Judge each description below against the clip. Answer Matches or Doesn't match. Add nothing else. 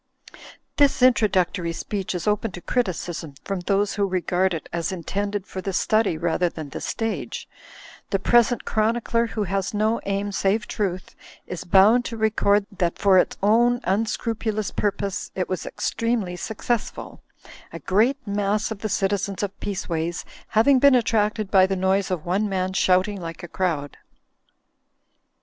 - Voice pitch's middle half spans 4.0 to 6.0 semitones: Doesn't match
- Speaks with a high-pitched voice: Matches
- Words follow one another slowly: Doesn't match